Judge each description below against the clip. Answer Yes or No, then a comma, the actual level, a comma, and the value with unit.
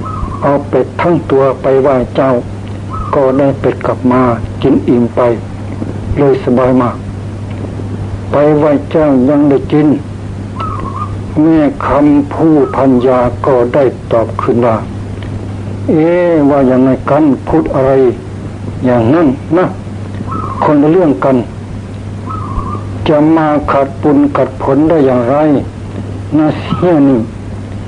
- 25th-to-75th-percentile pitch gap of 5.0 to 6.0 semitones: Yes, average, 5.3 semitones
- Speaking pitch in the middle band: No, low, 120 Hz